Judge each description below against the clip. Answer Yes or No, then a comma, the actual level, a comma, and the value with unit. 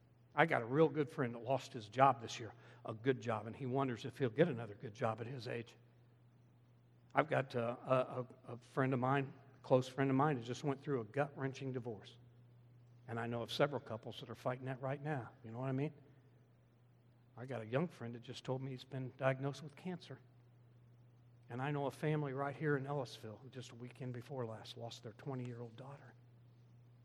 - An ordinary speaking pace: No, fast, 220 wpm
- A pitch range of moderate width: No, narrow, 2.1 semitones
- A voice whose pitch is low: Yes, low, 125 Hz